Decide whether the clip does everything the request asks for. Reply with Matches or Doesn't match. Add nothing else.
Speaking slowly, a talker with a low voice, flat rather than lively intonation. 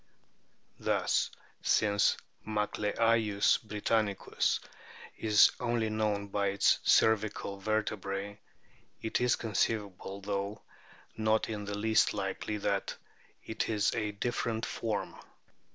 Matches